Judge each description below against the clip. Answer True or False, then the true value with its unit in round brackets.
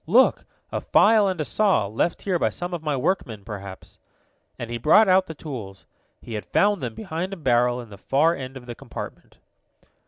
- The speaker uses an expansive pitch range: True (7.8 semitones)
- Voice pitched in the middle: True (150 Hz)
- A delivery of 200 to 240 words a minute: True (205 wpm)